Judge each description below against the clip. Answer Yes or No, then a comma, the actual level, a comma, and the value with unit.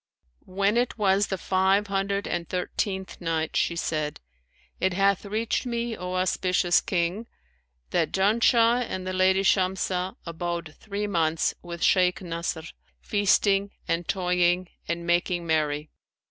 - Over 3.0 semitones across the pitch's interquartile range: No, narrow, 2.5 semitones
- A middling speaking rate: No, slow, 130 wpm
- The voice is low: No, medium, 185 Hz